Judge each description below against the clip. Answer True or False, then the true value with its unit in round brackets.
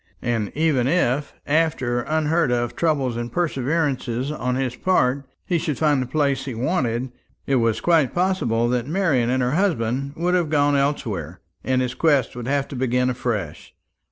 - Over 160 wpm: True (170 wpm)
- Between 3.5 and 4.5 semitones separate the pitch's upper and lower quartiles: True (4.1 semitones)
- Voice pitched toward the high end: False (135 Hz)